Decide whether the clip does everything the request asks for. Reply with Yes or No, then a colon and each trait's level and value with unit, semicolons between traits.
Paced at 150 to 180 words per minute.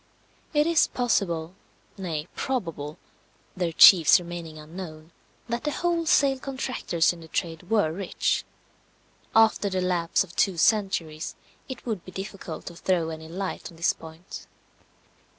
No: slow, 135 wpm